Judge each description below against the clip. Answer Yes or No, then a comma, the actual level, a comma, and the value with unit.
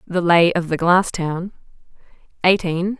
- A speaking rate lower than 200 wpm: Yes, average, 140 wpm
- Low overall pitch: No, medium, 175 Hz